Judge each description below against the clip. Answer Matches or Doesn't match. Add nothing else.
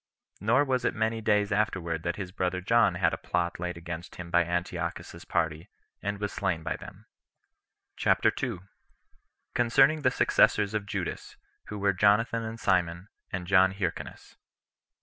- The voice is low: Matches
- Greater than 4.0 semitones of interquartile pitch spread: Doesn't match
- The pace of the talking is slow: Doesn't match